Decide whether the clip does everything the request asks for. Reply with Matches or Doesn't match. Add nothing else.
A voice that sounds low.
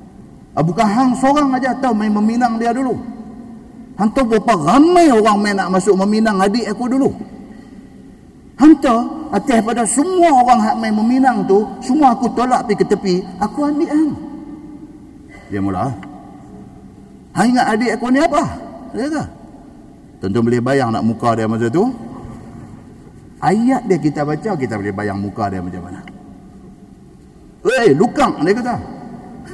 Doesn't match